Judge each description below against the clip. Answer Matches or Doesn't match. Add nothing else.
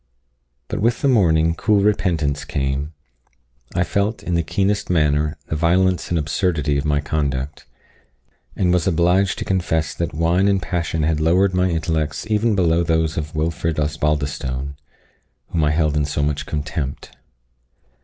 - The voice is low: Matches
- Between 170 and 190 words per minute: Doesn't match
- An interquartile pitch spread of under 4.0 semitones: Matches